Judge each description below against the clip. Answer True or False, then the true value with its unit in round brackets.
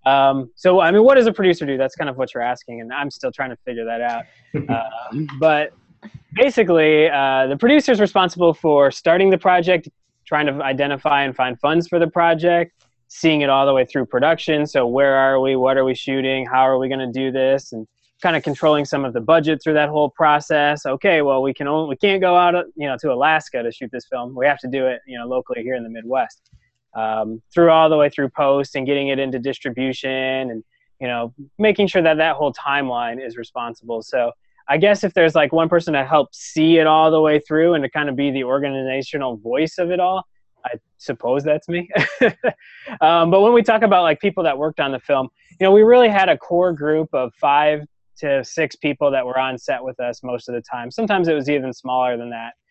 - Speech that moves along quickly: True (230 wpm)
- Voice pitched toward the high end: False (145 Hz)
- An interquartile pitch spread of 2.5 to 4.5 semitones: True (4.0 semitones)